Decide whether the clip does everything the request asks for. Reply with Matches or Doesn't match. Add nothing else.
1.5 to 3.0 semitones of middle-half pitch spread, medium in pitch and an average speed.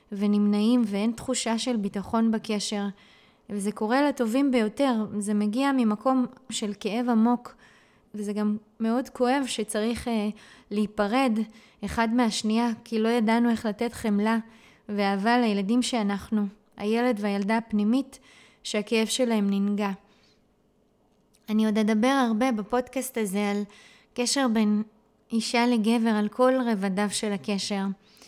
Doesn't match